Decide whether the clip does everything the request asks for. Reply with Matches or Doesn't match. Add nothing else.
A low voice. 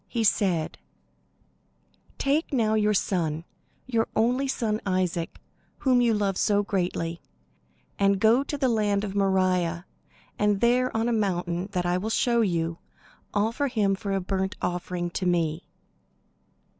Doesn't match